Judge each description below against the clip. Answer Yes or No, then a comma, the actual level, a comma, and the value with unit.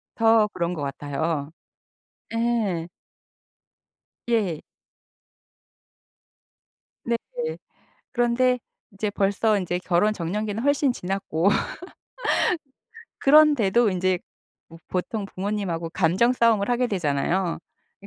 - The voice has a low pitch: No, high, 200 Hz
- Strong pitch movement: No, average, 5.0 semitones